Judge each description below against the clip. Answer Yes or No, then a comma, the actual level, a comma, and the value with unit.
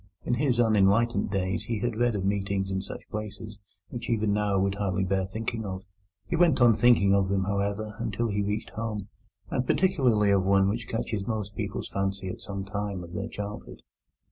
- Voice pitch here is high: No, low, 105 Hz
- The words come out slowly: No, average, 195 wpm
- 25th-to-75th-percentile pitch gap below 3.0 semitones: Yes, narrow, 2.6 semitones